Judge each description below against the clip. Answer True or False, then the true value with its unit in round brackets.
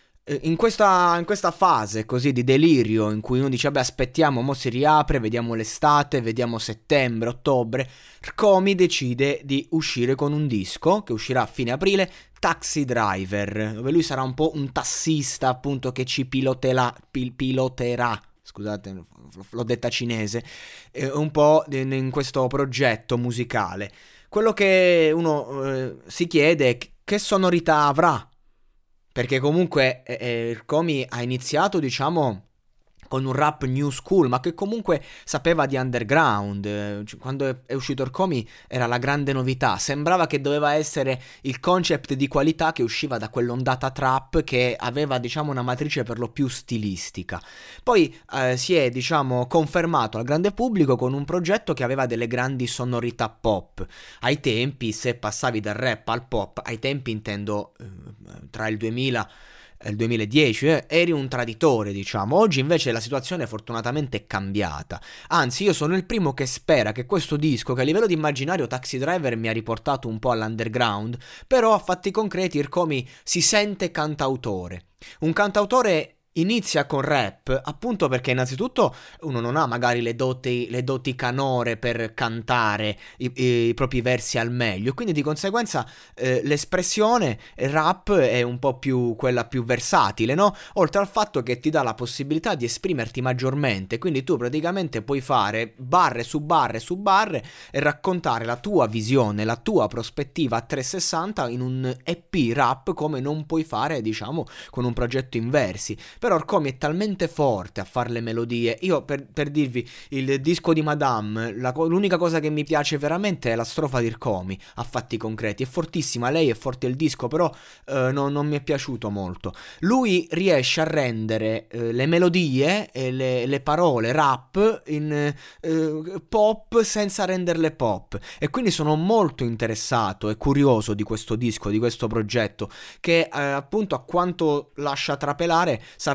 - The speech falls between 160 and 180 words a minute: True (165 wpm)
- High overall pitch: False (135 Hz)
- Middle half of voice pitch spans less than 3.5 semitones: False (4.8 semitones)